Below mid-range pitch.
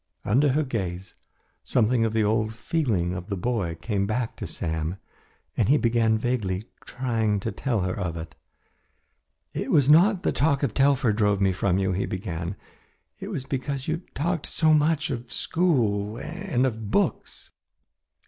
Yes: low, 115 Hz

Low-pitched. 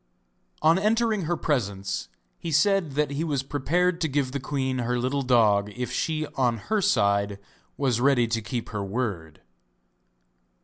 Yes: low, 130 Hz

